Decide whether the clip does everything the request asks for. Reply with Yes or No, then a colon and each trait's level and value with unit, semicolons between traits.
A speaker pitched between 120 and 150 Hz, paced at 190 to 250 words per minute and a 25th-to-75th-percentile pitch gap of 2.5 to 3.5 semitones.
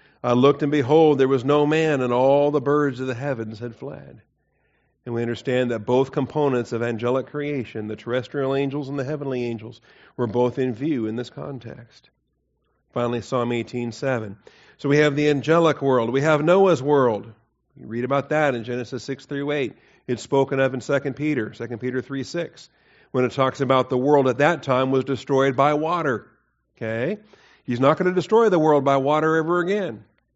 Yes: low, 135 Hz; average, 195 wpm; average, 3.2 semitones